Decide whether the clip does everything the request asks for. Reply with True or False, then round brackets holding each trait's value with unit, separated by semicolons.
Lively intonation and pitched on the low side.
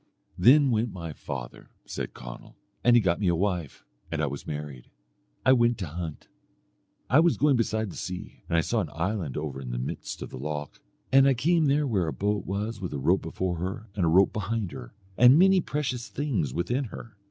True (7.1 semitones; 95 Hz)